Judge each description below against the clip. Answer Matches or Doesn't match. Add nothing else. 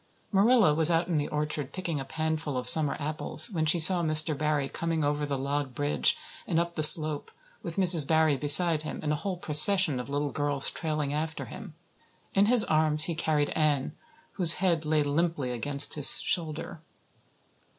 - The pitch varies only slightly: Matches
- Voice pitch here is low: Doesn't match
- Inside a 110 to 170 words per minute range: Doesn't match